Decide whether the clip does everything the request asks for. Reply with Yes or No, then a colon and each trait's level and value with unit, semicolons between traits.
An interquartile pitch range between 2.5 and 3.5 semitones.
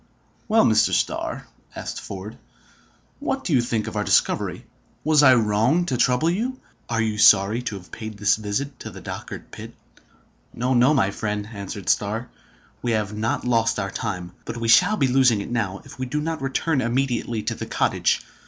No: average, 4.2 semitones